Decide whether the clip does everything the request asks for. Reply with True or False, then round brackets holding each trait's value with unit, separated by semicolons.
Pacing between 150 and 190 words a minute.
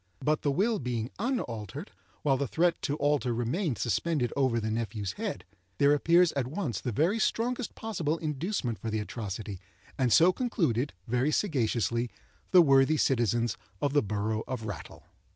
True (160 wpm)